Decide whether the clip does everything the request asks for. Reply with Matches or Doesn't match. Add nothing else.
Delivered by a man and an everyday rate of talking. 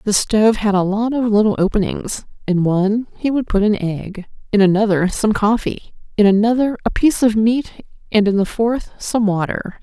Doesn't match